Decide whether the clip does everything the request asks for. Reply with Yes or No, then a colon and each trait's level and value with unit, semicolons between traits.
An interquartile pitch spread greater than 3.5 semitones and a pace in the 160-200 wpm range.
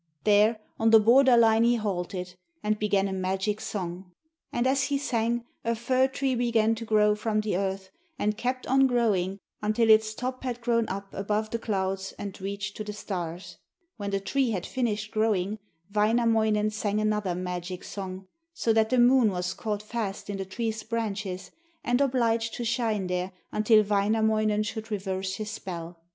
No: average, 2.9 semitones; average, 175 wpm